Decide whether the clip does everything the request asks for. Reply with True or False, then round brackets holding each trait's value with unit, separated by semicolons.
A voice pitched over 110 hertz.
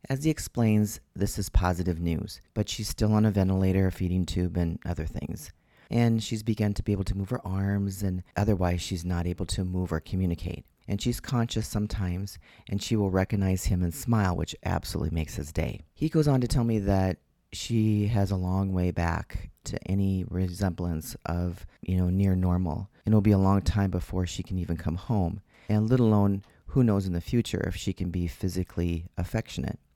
False (95 Hz)